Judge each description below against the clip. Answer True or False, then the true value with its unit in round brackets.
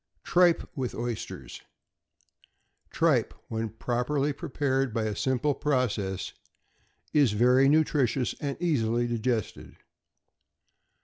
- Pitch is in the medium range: False (125 Hz)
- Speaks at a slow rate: True (90 wpm)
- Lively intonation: False (4.1 semitones)